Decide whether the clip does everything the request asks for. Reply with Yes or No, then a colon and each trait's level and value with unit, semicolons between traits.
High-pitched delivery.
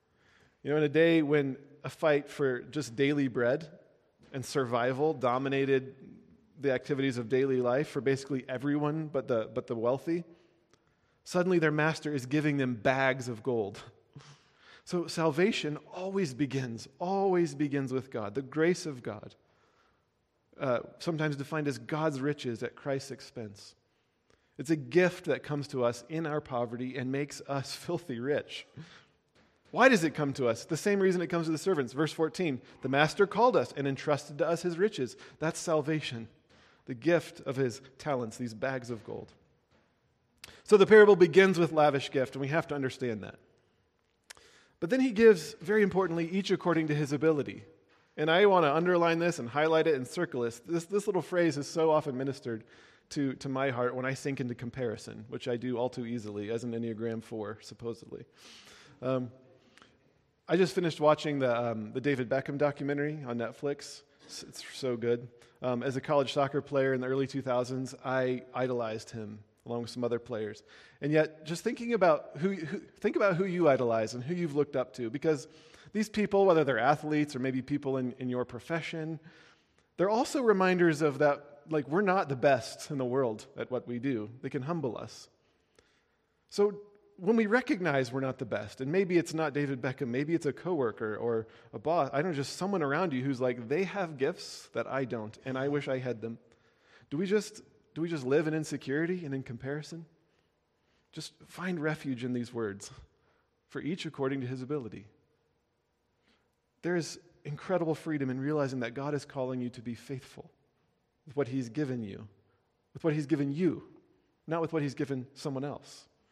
No: medium, 140 Hz